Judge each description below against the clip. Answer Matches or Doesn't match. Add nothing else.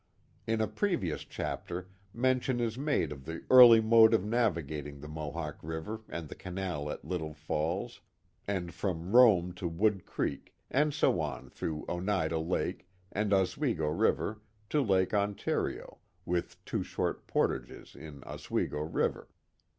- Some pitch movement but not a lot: Doesn't match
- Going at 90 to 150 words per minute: Matches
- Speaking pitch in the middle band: Doesn't match